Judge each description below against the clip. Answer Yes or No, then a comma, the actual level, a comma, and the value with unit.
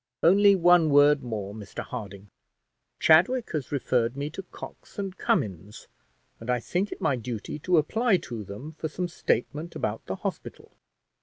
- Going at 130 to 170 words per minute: Yes, average, 160 wpm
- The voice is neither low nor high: Yes, medium, 145 Hz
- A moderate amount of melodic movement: No, wide, 7.6 semitones